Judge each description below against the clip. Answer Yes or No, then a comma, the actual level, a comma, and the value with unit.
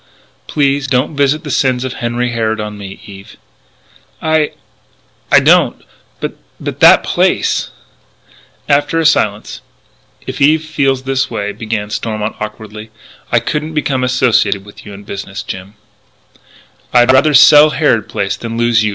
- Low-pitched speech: Yes, low, 120 Hz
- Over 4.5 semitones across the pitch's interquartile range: Yes, average, 4.9 semitones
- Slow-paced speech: No, average, 150 wpm